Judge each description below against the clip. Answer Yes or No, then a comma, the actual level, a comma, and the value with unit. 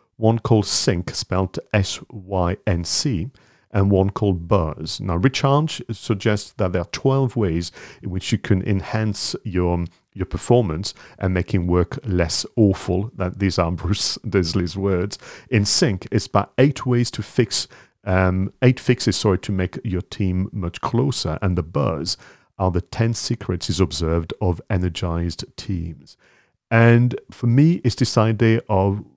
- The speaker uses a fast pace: No, average, 150 wpm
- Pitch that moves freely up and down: No, average, 3.9 semitones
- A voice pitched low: Yes, low, 100 Hz